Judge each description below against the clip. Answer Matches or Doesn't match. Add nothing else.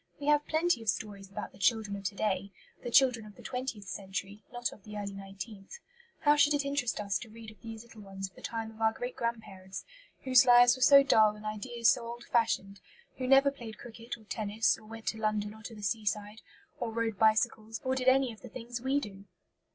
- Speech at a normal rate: Doesn't match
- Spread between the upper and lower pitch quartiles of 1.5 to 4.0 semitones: Matches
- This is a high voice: Matches